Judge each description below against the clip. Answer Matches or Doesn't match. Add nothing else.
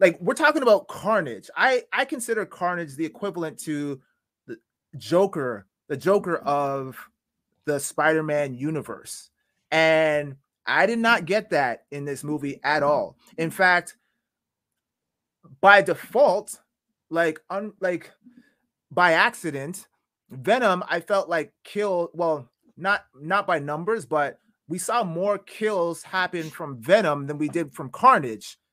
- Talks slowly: Matches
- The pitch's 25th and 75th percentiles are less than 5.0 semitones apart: Doesn't match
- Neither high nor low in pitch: Matches